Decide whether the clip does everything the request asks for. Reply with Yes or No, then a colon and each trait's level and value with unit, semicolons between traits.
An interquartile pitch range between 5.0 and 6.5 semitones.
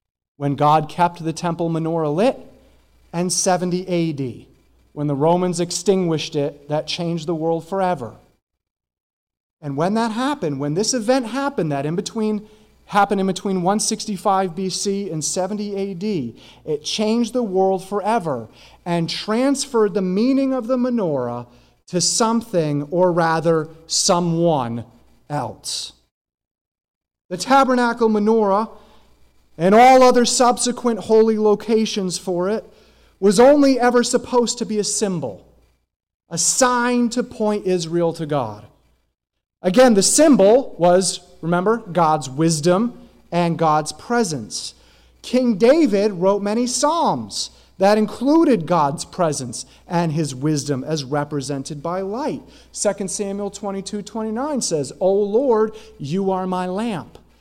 Yes: wide, 5.5 semitones